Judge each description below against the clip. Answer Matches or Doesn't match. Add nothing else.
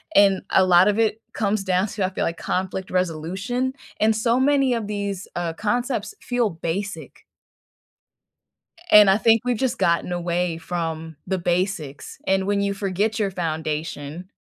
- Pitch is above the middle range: Matches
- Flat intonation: Doesn't match